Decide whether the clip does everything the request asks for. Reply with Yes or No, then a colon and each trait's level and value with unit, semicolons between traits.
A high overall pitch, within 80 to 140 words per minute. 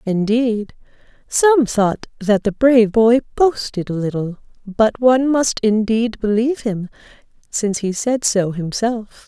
Yes: high, 225 Hz; slow, 135 wpm